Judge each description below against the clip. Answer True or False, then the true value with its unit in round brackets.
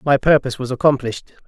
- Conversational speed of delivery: True (160 wpm)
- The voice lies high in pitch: False (135 Hz)